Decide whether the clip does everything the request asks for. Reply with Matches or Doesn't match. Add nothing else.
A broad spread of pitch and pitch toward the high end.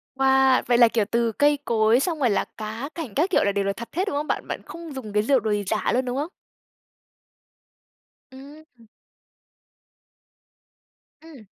Doesn't match